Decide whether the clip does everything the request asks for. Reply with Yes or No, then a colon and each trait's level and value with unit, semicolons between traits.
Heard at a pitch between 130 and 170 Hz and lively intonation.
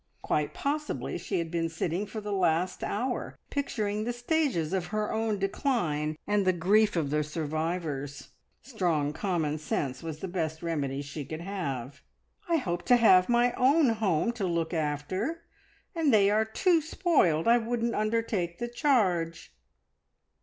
No: medium, 185 Hz; wide, 6.5 semitones